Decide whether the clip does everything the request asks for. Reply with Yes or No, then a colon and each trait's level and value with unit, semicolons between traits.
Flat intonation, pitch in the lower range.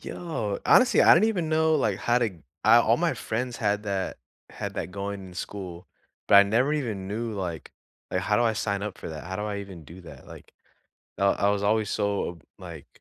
No: average, 3.4 semitones; low, 105 Hz